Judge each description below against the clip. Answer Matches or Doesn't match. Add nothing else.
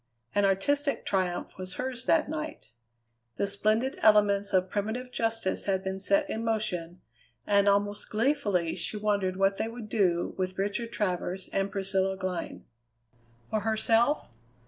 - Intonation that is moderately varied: Matches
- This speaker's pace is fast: Doesn't match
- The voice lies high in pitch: Matches